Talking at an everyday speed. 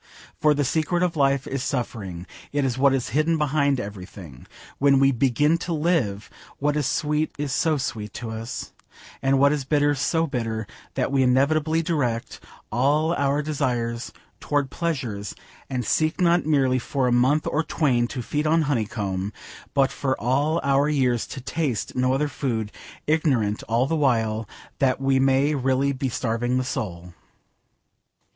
Yes: average, 165 wpm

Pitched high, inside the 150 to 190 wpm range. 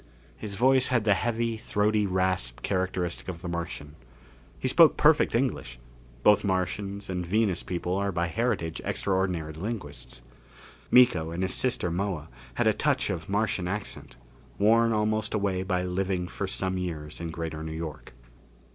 No: very low, 95 Hz; average, 155 wpm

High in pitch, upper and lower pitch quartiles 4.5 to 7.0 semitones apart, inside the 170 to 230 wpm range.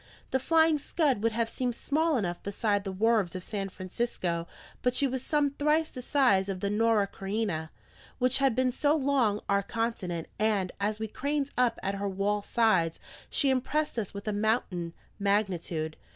Yes: high, 220 Hz; average, 4.9 semitones; average, 180 wpm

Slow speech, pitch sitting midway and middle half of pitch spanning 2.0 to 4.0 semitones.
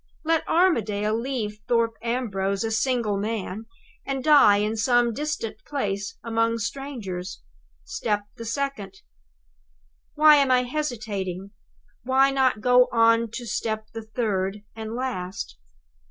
No: slow, 125 wpm; high, 230 Hz; average, 3.7 semitones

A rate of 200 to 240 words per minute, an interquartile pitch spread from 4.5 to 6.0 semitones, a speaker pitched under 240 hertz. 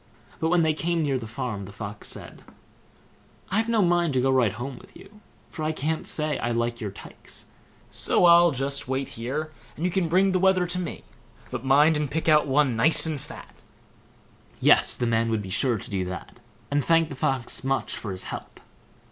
Yes: fast, 205 wpm; wide, 5.5 semitones; medium, 140 Hz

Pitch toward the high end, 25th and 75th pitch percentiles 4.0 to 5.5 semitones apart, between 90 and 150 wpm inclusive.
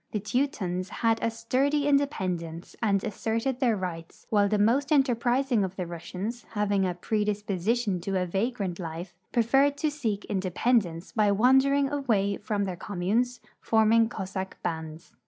Yes: high, 210 Hz; average, 4.7 semitones; average, 145 wpm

